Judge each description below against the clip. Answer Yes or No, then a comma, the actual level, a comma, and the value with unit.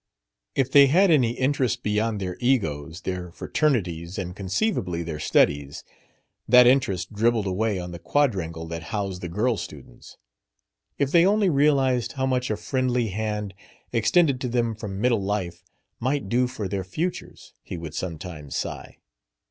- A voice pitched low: Yes, low, 110 Hz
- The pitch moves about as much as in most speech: No, wide, 6.2 semitones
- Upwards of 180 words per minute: No, average, 155 wpm